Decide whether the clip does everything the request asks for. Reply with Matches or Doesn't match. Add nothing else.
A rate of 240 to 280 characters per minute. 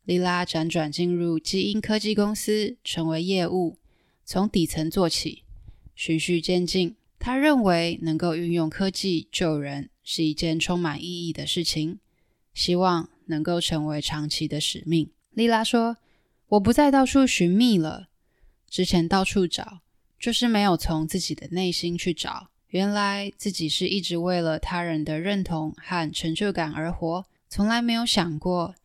Doesn't match